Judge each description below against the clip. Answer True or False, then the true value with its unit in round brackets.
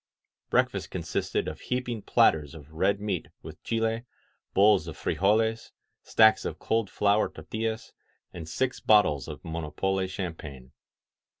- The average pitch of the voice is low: True (100 Hz)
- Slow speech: True (125 wpm)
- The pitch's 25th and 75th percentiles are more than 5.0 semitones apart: True (5.5 semitones)